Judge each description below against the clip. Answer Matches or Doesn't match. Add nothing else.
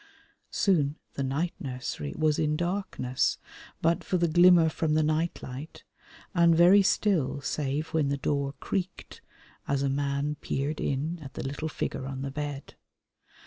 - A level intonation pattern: Doesn't match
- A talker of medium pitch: Matches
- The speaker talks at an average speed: Matches